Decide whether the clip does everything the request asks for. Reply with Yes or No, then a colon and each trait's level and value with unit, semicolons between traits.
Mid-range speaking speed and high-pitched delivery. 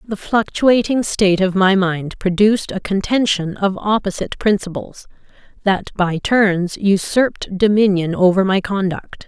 No: slow, 130 wpm; high, 195 Hz